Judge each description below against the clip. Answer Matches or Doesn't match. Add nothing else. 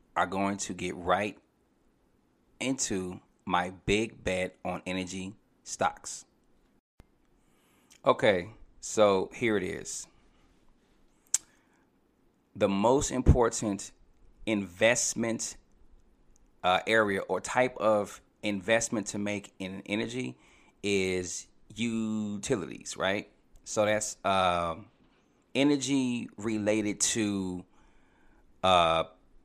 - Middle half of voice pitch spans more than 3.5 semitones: Doesn't match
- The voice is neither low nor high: Doesn't match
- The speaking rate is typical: Doesn't match